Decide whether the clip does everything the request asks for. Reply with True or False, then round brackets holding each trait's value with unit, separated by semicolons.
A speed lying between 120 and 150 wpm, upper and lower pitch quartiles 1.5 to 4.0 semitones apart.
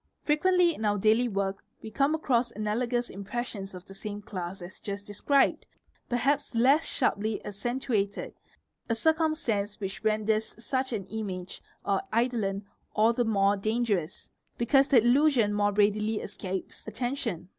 True (140 wpm; 3.5 semitones)